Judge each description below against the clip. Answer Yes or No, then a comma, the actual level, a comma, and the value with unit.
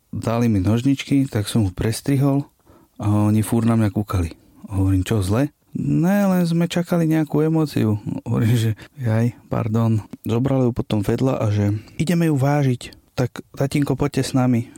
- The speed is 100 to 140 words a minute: No, average, 160 wpm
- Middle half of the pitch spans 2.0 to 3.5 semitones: No, average, 4.5 semitones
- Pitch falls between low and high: No, low, 120 Hz